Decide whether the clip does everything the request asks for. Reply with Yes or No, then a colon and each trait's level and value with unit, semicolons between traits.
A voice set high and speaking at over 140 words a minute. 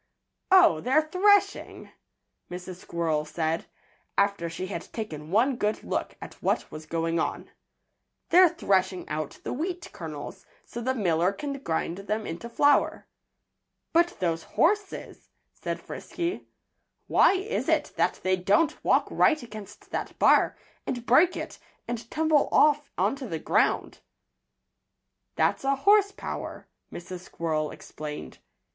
No: high, 210 Hz; slow, 135 wpm